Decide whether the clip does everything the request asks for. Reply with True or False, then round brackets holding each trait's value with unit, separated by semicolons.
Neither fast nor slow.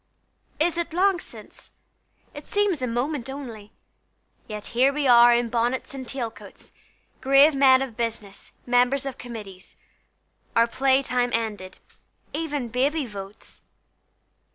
False (130 wpm)